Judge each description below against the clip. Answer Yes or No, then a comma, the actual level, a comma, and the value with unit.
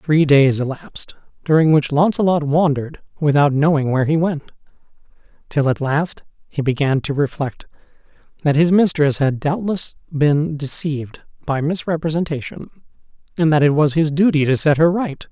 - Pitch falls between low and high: Yes, medium, 150 Hz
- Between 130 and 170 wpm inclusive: Yes, average, 150 wpm